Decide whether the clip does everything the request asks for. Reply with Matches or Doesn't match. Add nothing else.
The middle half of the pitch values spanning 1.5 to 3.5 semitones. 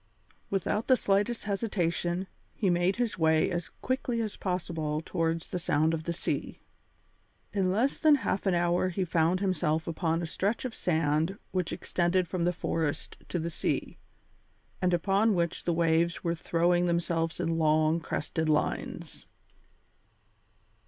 Matches